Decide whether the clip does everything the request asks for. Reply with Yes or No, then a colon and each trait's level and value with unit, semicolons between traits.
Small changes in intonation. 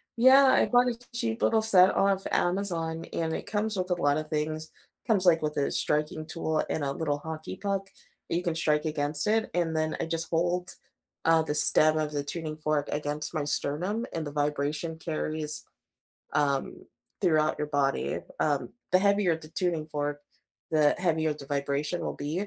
No: average, 3.1 semitones